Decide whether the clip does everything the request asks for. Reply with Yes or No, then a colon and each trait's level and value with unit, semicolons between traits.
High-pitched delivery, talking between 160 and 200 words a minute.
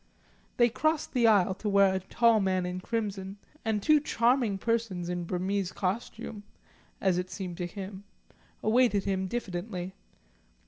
No: high, 200 Hz; average, 145 wpm